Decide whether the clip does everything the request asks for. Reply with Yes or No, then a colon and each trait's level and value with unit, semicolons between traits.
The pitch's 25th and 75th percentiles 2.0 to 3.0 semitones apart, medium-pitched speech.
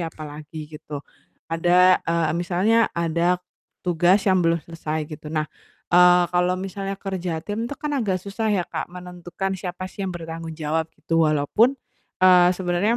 Yes: average, 2.7 semitones; medium, 175 Hz